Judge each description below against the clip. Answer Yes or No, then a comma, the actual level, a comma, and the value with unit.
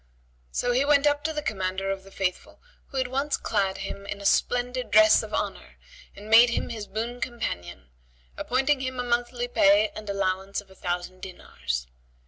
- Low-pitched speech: No, high, 215 Hz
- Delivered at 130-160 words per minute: No, average, 185 wpm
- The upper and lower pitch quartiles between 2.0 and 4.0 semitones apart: No, average, 4.5 semitones